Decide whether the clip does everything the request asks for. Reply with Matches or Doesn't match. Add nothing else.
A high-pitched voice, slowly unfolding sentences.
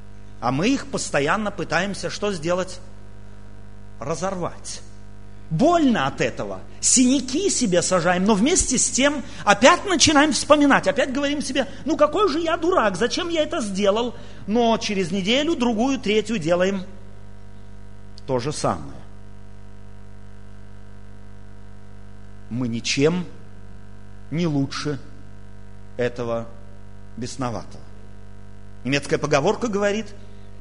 Doesn't match